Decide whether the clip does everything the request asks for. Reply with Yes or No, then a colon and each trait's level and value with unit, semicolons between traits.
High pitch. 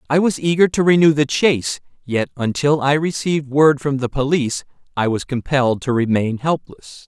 No: medium, 140 Hz